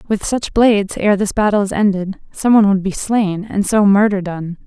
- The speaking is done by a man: No, female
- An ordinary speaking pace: No, fast, 220 wpm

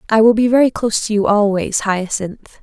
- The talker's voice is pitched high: Yes, high, 215 Hz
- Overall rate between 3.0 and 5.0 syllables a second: No, 5.4 syllables/s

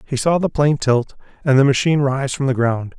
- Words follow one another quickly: Yes, fast, 240 wpm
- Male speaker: Yes, male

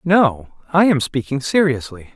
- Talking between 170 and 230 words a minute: No, average, 140 wpm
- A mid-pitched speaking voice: Yes, medium, 145 Hz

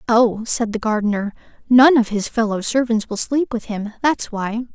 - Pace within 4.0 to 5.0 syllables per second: Yes, 4.7 syllables/s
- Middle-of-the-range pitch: No, high, 230 Hz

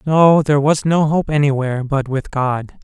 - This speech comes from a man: Yes, male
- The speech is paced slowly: No, average, 190 wpm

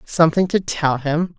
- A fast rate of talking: No, average, 175 wpm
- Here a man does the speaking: No, female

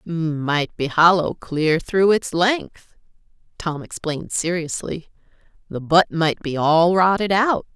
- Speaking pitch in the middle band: Yes, medium, 170 Hz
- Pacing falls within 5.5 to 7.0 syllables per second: No, 3.6 syllables/s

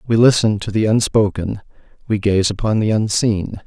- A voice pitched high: No, low, 105 Hz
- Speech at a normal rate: Yes, average, 165 wpm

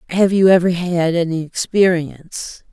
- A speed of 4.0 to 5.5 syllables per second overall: Yes, 4.5 syllables/s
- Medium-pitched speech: Yes, medium, 175 Hz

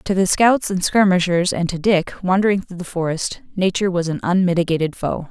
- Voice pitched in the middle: Yes, medium, 180 Hz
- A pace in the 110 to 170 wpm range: No, average, 190 wpm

